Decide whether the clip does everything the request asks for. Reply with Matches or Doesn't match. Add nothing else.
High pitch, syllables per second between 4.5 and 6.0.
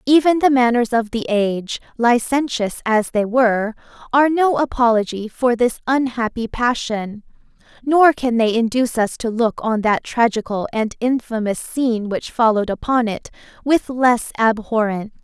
Matches